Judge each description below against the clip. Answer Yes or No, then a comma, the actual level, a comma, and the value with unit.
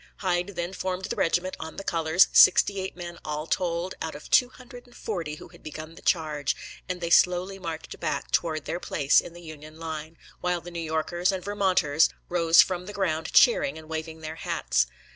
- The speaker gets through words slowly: No, average, 200 wpm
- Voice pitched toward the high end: No, medium, 170 Hz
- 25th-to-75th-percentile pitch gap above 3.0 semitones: No, narrow, 2.6 semitones